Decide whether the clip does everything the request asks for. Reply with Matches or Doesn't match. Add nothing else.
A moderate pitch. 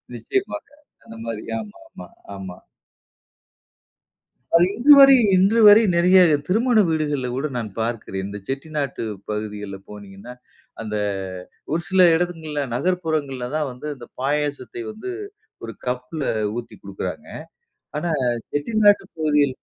Matches